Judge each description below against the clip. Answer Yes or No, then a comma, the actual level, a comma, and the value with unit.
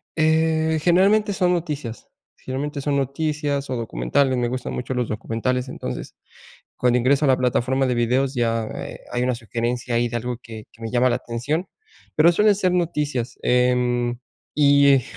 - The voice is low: Yes, low, 130 Hz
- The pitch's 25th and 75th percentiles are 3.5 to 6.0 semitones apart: Yes, average, 3.9 semitones